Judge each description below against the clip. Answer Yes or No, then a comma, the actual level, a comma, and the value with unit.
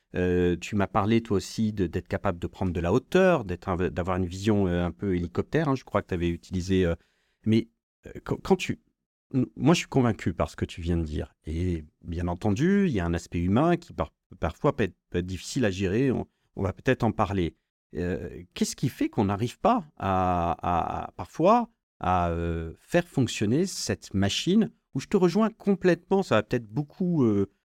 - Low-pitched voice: Yes, low, 100 Hz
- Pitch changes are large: Yes, wide, 8.7 semitones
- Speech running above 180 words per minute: Yes, average, 195 wpm